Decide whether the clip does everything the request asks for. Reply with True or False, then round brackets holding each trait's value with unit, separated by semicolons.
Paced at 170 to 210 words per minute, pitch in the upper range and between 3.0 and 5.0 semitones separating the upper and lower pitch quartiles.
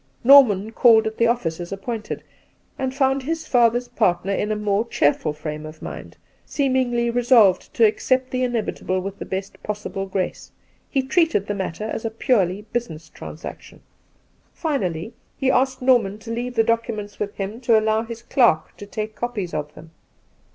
True (175 wpm; 220 Hz; 4.0 semitones)